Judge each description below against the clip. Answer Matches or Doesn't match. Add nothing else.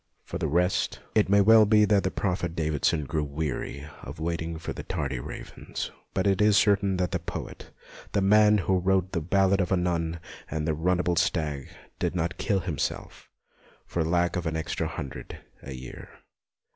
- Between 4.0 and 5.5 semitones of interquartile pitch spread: Doesn't match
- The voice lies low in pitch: Matches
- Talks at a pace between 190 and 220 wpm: Matches